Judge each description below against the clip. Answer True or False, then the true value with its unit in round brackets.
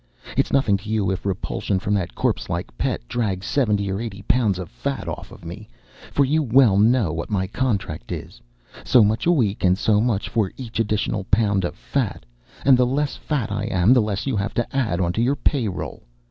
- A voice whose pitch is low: True (105 Hz)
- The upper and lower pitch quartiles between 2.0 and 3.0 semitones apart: False (4.3 semitones)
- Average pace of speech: False (215 wpm)